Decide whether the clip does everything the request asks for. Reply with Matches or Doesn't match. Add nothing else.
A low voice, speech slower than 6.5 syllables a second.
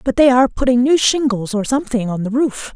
Doesn't match